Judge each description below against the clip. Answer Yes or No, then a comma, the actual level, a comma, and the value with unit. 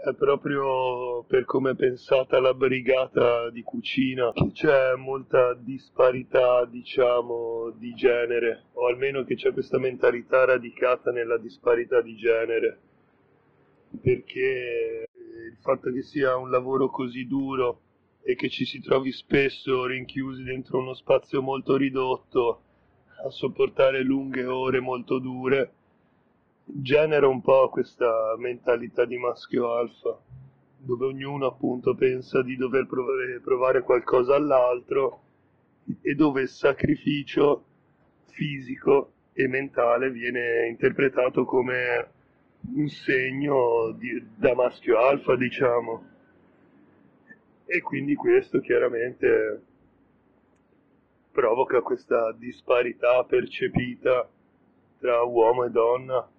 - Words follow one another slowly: Yes, slow, 105 wpm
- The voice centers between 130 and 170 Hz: Yes, low, 135 Hz